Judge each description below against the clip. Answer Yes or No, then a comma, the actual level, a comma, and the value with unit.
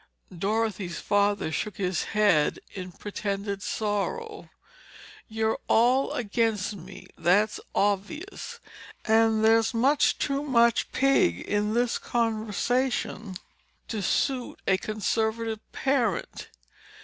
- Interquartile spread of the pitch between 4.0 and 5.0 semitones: No, average, 2.9 semitones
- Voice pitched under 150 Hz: No, high, 220 Hz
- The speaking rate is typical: No, slow, 100 wpm